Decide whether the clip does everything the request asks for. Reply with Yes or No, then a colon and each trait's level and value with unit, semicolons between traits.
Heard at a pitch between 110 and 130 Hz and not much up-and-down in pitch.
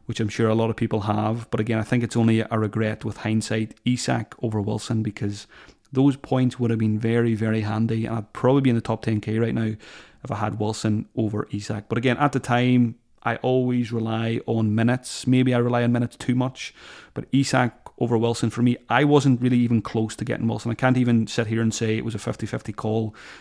Yes: low, 115 Hz; narrow, 1.9 semitones